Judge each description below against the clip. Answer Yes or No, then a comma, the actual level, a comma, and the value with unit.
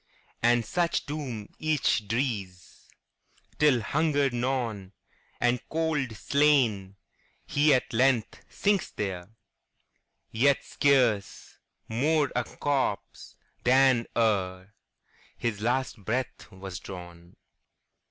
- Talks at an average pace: No, slow, 80 wpm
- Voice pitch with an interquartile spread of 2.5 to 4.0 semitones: No, average, 5.3 semitones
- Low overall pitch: Yes, low, 120 Hz